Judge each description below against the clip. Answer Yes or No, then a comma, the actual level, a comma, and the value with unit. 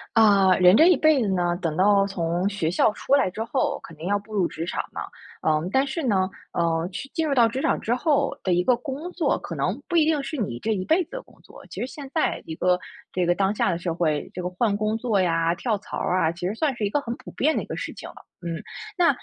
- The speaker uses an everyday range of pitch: No, wide, 7.0 semitones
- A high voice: Yes, high, 200 Hz